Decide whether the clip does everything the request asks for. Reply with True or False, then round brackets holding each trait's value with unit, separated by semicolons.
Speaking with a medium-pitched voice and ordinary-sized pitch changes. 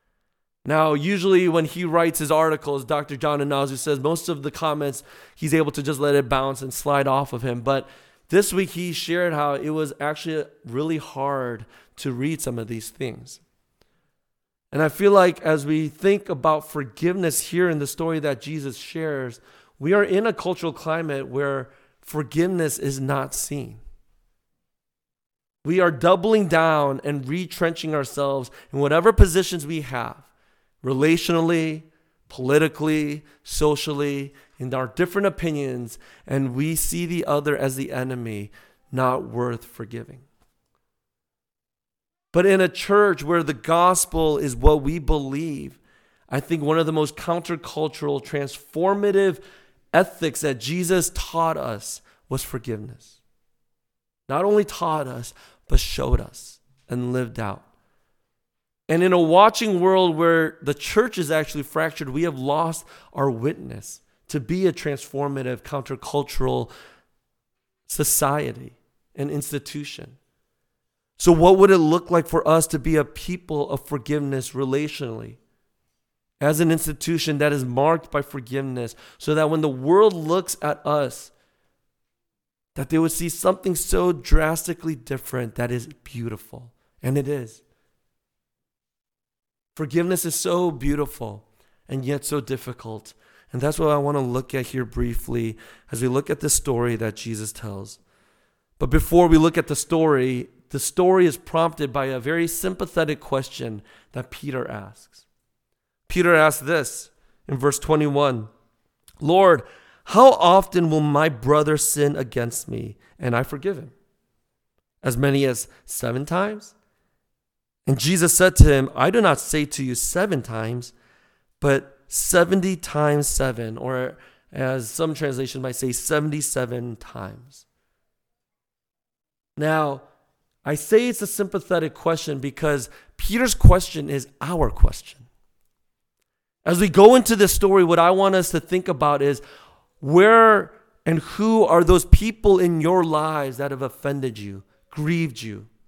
True (150 Hz; 3.9 semitones)